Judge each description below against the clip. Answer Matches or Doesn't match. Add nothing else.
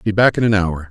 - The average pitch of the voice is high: Doesn't match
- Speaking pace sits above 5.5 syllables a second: Matches